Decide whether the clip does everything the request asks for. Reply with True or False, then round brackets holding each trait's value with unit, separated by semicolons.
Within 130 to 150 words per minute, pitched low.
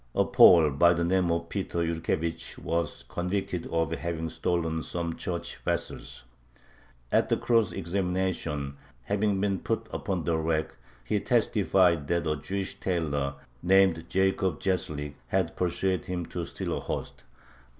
True (140 wpm; 85 Hz)